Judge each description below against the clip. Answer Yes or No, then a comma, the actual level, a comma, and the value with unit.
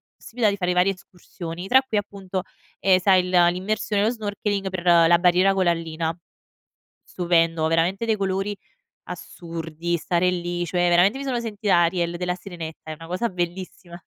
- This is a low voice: No, medium, 180 Hz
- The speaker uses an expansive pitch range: No, narrow, 2.5 semitones